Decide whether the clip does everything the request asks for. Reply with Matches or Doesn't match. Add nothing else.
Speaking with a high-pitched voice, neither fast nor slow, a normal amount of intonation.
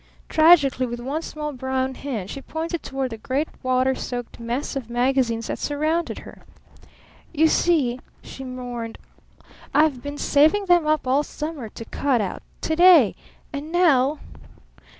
Matches